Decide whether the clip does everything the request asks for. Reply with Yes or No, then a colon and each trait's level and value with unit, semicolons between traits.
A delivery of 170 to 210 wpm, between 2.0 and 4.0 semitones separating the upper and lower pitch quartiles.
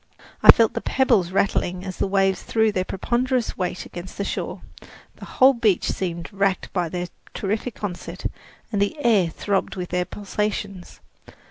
No: average, 160 wpm; average, 2.9 semitones